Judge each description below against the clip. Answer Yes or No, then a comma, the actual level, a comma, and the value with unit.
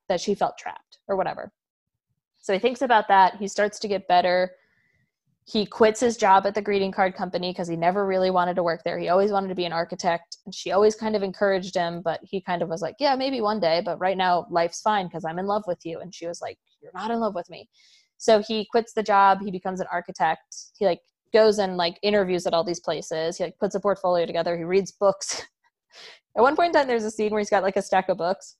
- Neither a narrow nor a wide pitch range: Yes, average, 3.0 semitones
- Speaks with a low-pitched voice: No, high, 190 Hz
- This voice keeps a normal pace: No, fast, 255 wpm